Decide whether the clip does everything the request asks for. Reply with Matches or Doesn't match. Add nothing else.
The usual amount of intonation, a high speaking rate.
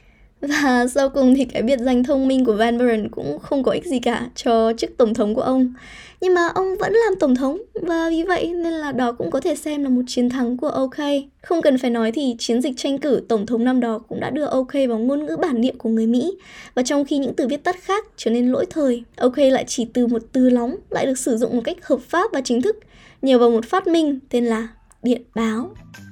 Matches